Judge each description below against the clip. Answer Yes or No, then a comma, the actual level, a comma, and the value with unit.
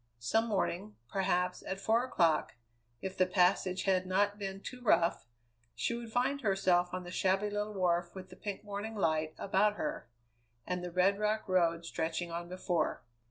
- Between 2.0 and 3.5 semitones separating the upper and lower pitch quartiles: Yes, average, 2.8 semitones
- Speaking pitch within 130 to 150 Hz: No, high, 190 Hz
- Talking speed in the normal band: Yes, average, 170 wpm